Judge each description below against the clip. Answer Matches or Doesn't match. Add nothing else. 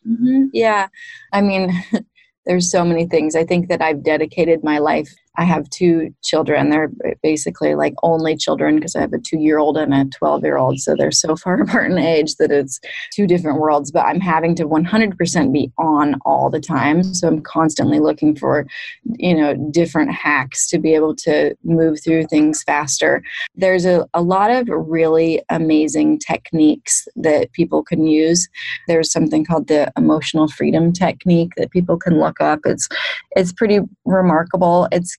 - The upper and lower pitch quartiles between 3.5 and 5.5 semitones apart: Doesn't match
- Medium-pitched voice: Matches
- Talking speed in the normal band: Matches